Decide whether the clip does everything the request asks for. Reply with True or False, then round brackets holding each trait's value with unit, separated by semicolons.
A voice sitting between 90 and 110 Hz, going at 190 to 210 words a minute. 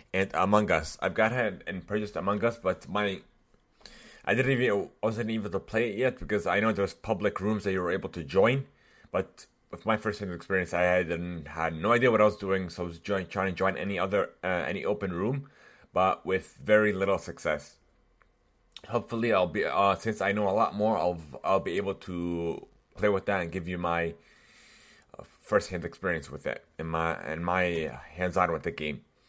True (95 Hz; 205 wpm)